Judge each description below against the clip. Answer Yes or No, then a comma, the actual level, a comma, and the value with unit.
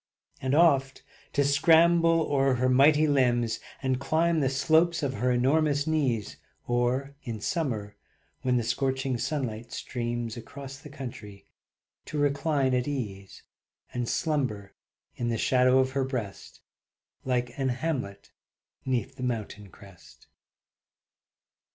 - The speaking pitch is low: Yes, low, 130 Hz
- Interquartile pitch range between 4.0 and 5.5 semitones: No, average, 3.1 semitones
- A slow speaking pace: Yes, slow, 125 wpm